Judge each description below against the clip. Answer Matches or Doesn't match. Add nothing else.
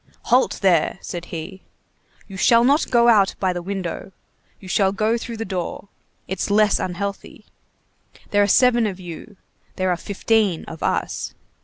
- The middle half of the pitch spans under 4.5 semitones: Matches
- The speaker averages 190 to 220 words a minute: Doesn't match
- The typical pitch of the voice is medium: Doesn't match